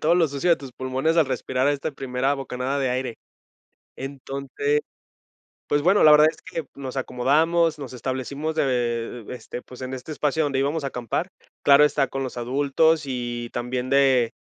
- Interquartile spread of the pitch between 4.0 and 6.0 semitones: No, narrow, 2.6 semitones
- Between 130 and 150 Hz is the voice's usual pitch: Yes, low, 135 Hz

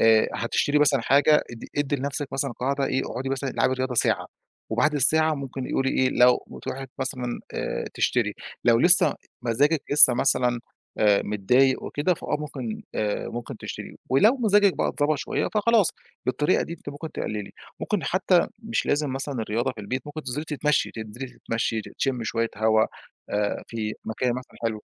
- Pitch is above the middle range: No, low, 135 Hz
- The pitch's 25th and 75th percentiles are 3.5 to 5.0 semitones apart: Yes, average, 4.1 semitones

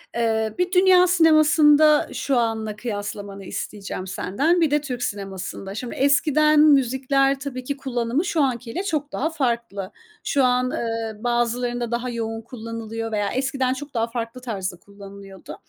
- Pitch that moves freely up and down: No, average, 4.2 semitones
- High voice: Yes, high, 245 Hz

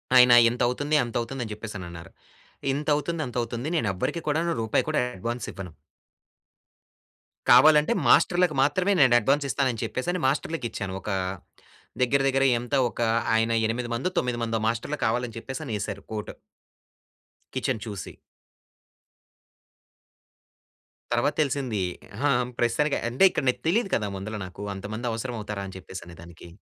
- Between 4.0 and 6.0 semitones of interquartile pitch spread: Yes, average, 4.9 semitones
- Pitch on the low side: Yes, low, 120 Hz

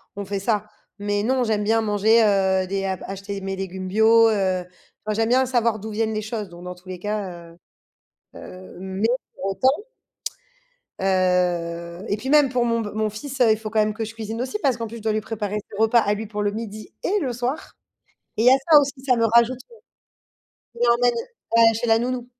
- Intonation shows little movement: No, average, 3.1 semitones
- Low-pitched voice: No, high, 215 Hz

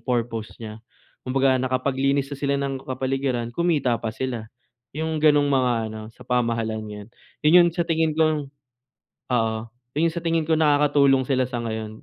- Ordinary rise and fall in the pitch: Yes, average, 3.9 semitones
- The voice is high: No, low, 135 Hz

